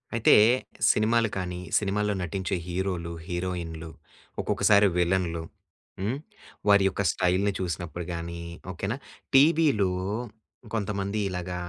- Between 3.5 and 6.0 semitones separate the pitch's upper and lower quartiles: No, average, 2.7 semitones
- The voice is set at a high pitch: No, very low, 95 Hz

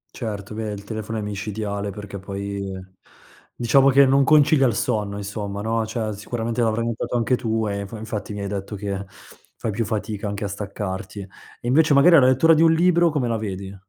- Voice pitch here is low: Yes, low, 110 Hz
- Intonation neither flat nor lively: Yes, average, 3.4 semitones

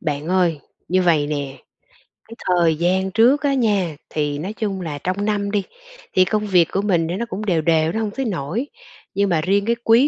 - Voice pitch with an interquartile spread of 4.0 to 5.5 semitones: Yes, average, 4.4 semitones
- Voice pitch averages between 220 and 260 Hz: No, medium, 185 Hz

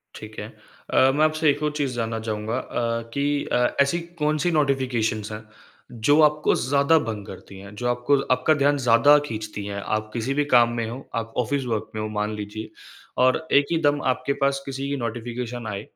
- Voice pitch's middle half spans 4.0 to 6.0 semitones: Yes, average, 4.3 semitones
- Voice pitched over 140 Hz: No, low, 125 Hz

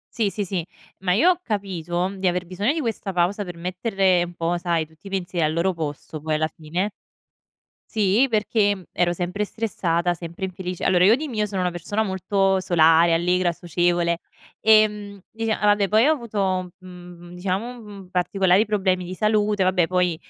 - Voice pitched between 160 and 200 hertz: Yes, medium, 185 Hz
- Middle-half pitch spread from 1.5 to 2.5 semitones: No, average, 2.9 semitones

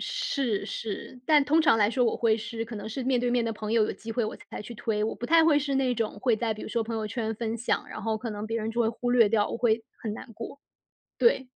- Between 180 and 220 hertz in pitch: No, high, 230 Hz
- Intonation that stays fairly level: Yes, narrow, 2.2 semitones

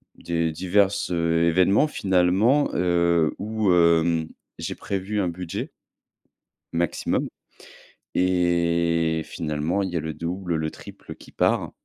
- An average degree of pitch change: No, narrow, 2.1 semitones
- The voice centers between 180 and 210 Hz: No, very low, 85 Hz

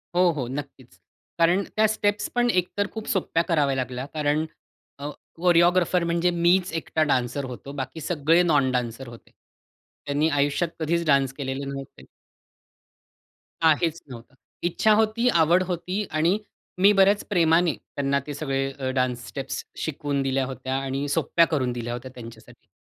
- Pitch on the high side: No, medium, 150 Hz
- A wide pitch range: No, average, 4.5 semitones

